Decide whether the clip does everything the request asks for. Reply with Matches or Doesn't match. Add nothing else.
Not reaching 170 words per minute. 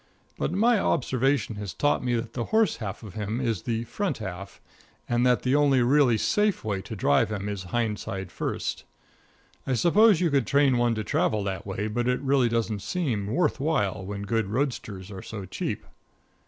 Doesn't match